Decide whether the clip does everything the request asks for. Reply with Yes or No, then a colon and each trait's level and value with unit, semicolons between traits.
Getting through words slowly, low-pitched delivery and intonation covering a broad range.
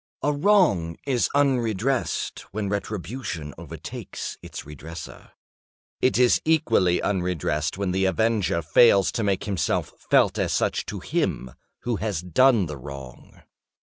Yes: slow, 130 wpm; low, 100 Hz; wide, 6.4 semitones